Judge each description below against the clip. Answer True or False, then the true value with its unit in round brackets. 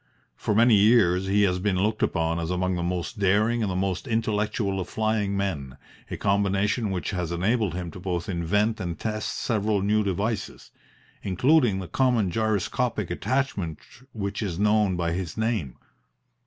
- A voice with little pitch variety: False (3.1 semitones)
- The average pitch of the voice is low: True (100 Hz)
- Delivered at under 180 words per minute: True (165 wpm)